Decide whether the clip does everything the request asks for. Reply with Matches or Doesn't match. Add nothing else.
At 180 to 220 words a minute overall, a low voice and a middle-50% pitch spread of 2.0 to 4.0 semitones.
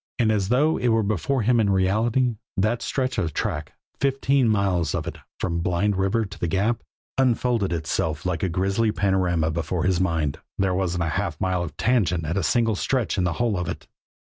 Doesn't match